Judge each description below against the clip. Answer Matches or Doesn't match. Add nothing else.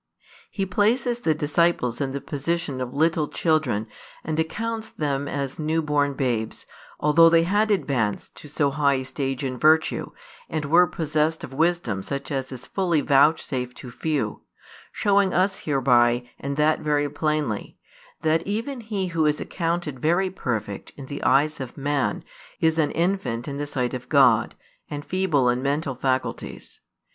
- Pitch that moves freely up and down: Doesn't match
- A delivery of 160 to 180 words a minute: Matches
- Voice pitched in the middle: Matches